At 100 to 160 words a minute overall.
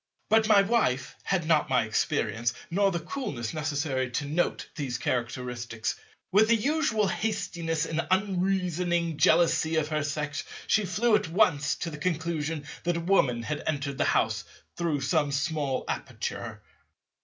Yes: average, 150 wpm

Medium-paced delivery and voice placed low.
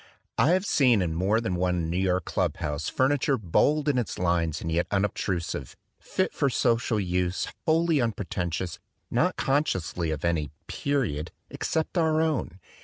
Yes: average, 170 wpm; very low, 95 Hz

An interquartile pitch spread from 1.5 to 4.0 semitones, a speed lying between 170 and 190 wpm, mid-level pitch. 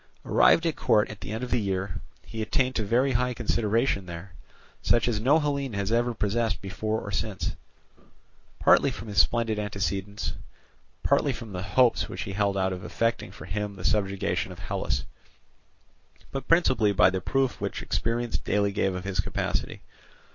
No: average, 3.4 semitones; average, 175 wpm; low, 105 Hz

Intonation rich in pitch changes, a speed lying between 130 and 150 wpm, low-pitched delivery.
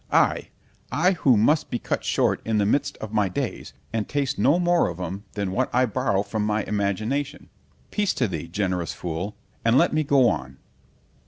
No: wide, 6.0 semitones; average, 180 wpm; low, 110 Hz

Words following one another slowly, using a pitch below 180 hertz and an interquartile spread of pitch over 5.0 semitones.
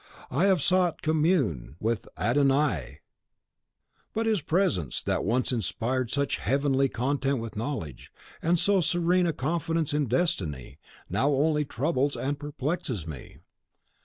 Yes: slow, 130 wpm; medium, 140 Hz; wide, 5.6 semitones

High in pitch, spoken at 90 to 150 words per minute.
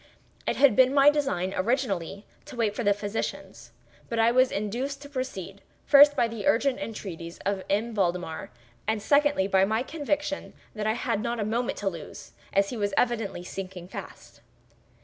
No: high, 220 Hz; average, 175 wpm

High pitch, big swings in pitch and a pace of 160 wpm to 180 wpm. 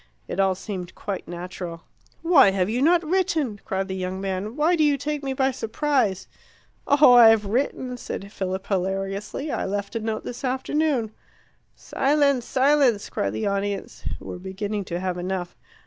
Yes: high, 210 Hz; wide, 6.2 semitones; average, 165 wpm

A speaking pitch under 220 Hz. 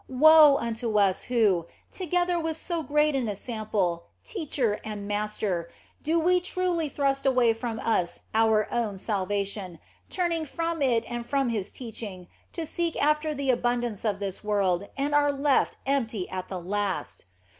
No: high, 235 Hz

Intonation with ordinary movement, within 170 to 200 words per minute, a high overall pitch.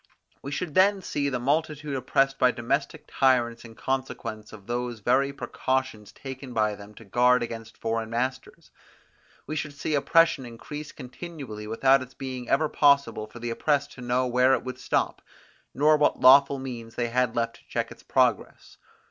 No: average, 3.2 semitones; average, 175 wpm; low, 130 Hz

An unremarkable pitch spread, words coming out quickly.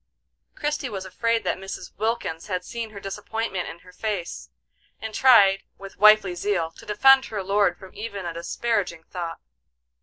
No: average, 3.5 semitones; average, 160 wpm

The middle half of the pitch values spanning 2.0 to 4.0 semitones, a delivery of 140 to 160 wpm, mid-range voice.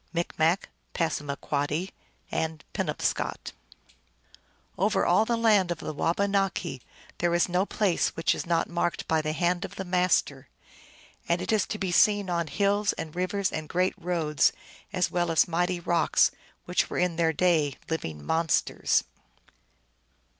Yes: average, 2.7 semitones; average, 150 wpm; medium, 175 Hz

